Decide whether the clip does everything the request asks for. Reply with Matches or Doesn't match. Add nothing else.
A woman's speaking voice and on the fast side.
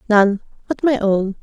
Doesn't match